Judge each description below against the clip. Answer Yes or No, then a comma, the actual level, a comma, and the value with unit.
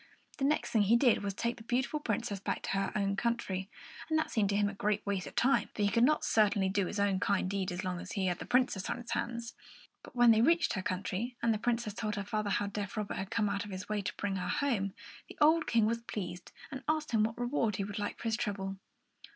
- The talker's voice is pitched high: Yes, high, 210 Hz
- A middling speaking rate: No, fast, 265 wpm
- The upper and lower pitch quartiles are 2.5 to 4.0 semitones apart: Yes, average, 3.1 semitones